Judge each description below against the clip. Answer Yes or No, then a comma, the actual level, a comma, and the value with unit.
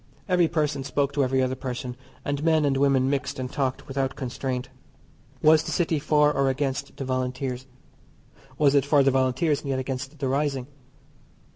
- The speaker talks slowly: No, average, 175 wpm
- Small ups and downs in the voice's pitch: Yes, narrow, 1.9 semitones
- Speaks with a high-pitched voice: No, low, 135 Hz